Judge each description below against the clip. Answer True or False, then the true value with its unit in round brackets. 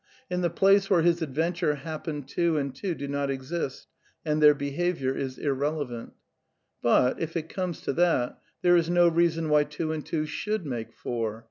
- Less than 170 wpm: False (195 wpm)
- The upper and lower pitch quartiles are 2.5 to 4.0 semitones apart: True (3.7 semitones)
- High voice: False (155 Hz)